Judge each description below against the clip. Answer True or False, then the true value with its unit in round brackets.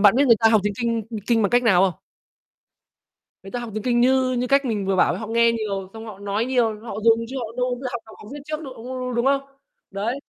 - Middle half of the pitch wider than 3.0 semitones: False (2.7 semitones)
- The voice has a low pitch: False (230 Hz)